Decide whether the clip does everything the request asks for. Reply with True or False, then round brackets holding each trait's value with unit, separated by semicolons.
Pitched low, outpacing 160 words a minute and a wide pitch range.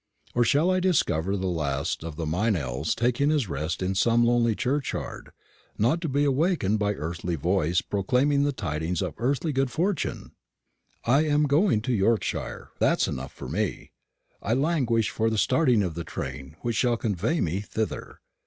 True (115 Hz; 170 wpm; 7.8 semitones)